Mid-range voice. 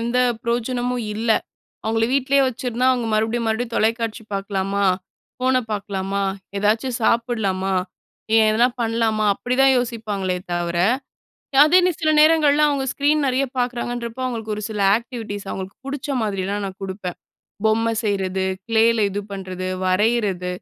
No: high, 225 Hz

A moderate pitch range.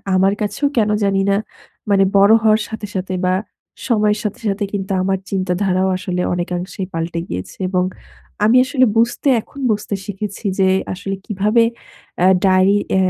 No: narrow, 2.1 semitones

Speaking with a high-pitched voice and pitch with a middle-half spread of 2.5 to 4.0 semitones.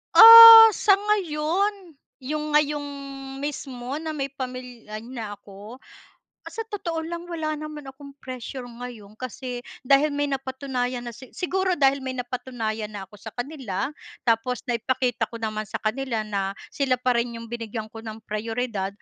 No: very high, 255 Hz; average, 4.8 semitones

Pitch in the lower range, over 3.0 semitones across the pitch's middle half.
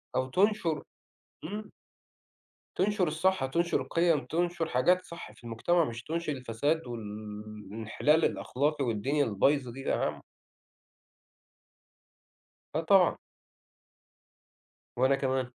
No: medium, 150 Hz; average, 5.1 semitones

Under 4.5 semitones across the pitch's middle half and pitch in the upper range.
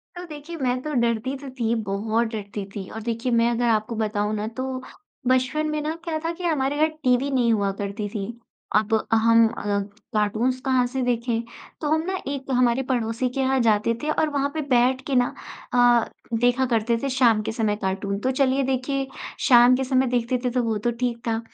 Yes: average, 3.0 semitones; high, 245 Hz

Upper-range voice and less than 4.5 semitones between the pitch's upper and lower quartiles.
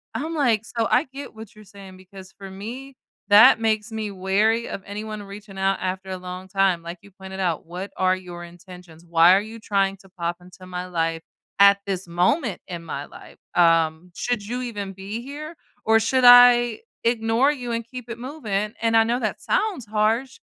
Yes: high, 200 Hz; average, 3.9 semitones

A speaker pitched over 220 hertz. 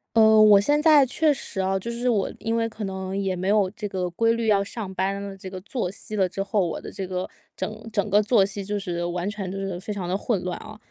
No: high, 200 Hz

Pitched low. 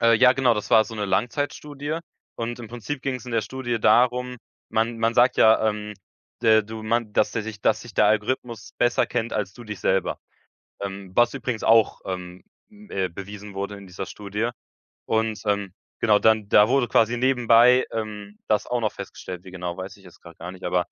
Yes: low, 110 Hz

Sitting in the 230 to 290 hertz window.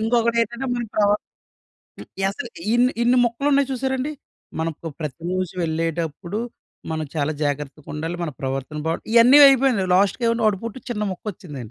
No: high, 200 Hz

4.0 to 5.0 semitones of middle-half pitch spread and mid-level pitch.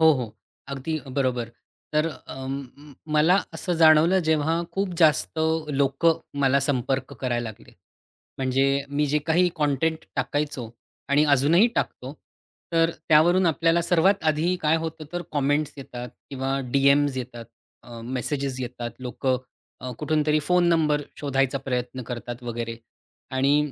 No: average, 3.6 semitones; medium, 145 Hz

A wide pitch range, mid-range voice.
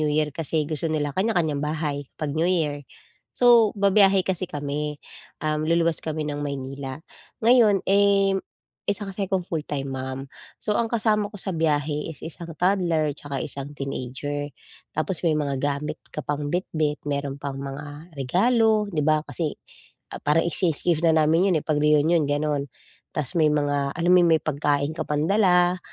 No: average, 3.6 semitones; medium, 155 Hz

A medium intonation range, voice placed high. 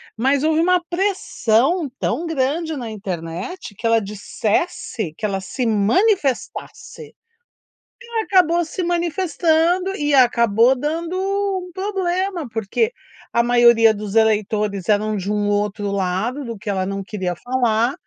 No: wide, 8.6 semitones; high, 245 Hz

